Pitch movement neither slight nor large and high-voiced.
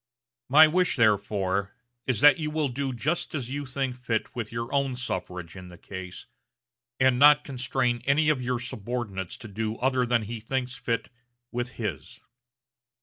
No: average, 4.0 semitones; low, 125 Hz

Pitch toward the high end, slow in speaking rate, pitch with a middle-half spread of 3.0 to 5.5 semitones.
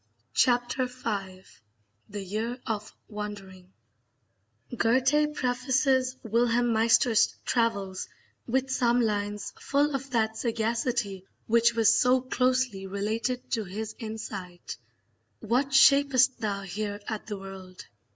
Yes: high, 225 Hz; slow, 110 wpm; average, 3.6 semitones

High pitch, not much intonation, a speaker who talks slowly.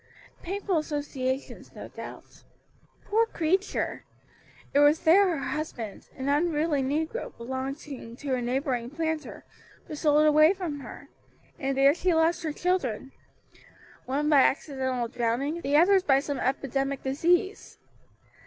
No: very high, 290 Hz; average, 3.6 semitones; slow, 130 wpm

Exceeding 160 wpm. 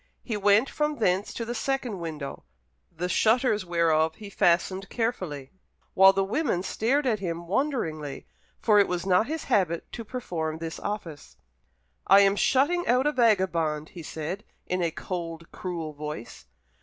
No: average, 155 wpm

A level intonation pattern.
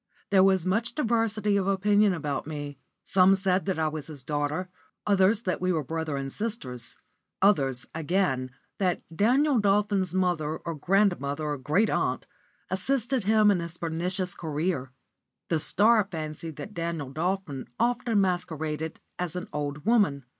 No: average, 4.8 semitones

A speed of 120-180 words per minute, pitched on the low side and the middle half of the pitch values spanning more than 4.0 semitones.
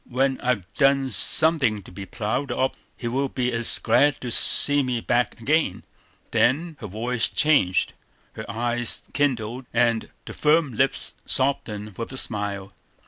No: average, 150 wpm; low, 120 Hz; average, 3.7 semitones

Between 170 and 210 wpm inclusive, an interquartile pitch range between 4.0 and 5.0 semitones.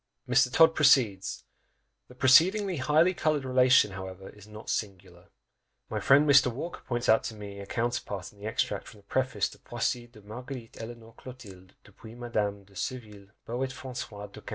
Yes: average, 175 wpm; average, 4.3 semitones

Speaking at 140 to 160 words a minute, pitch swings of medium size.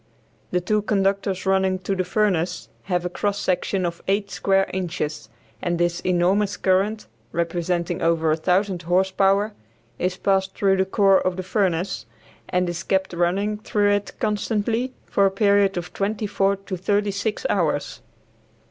No: average, 155 wpm; narrow, 2.3 semitones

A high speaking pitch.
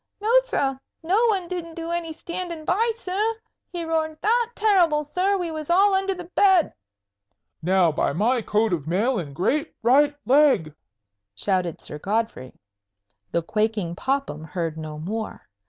Yes: very high, 295 Hz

